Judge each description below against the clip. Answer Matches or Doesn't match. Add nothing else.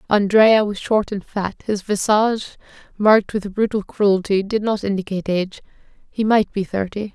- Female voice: Matches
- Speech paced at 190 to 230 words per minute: Doesn't match